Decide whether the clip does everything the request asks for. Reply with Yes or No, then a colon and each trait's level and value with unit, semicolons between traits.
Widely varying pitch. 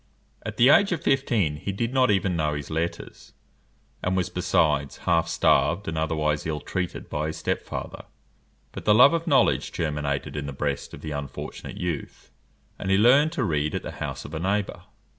Yes: wide, 5.7 semitones